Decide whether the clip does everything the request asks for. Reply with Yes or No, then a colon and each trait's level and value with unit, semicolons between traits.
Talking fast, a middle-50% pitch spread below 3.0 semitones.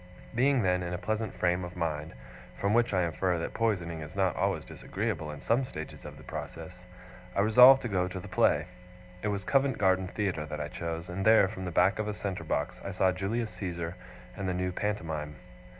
No: fast, 215 wpm; average, 3.6 semitones